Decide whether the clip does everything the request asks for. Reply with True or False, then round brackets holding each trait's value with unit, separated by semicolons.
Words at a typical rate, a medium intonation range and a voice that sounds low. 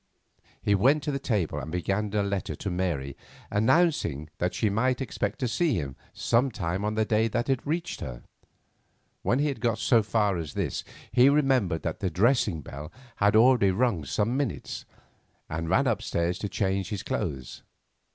False (175 wpm; 6.1 semitones; 105 Hz)